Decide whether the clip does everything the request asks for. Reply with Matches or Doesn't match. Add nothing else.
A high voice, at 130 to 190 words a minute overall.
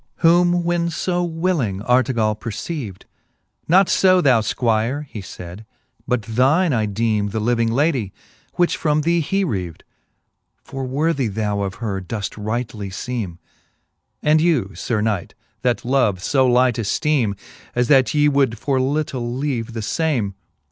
Doesn't match